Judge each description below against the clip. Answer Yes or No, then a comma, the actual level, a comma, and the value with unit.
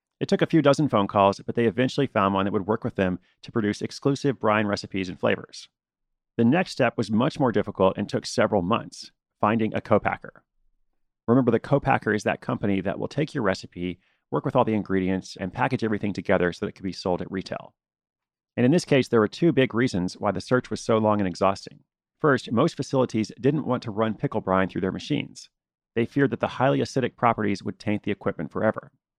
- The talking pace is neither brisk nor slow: No, fast, 220 wpm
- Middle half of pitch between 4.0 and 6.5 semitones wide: Yes, average, 4.4 semitones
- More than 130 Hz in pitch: No, low, 110 Hz